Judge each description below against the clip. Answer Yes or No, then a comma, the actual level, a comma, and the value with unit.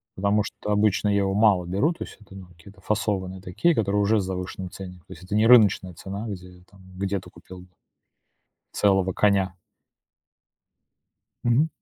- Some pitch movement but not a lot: No, narrow, 2.1 semitones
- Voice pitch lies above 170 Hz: No, low, 100 Hz